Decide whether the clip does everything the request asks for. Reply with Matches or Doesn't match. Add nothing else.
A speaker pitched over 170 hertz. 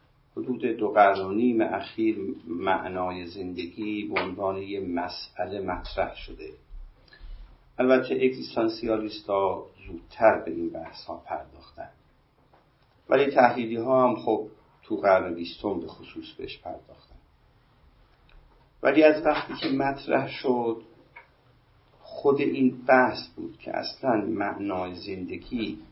Doesn't match